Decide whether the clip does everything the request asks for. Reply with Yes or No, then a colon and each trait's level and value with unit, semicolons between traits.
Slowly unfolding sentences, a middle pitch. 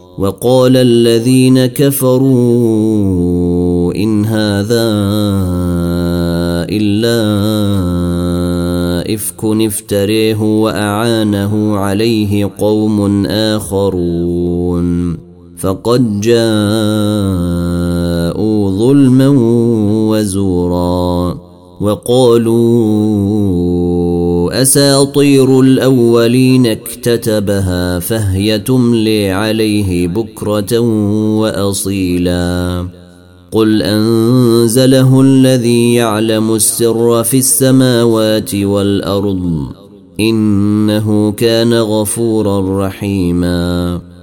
No: slow, 50 wpm; low, 105 Hz